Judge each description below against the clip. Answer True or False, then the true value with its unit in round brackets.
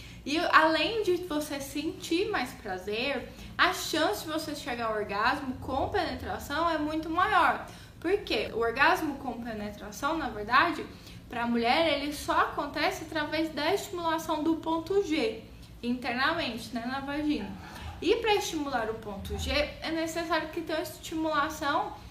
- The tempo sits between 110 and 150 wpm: True (145 wpm)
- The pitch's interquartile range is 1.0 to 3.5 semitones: False (4.0 semitones)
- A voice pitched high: True (310 Hz)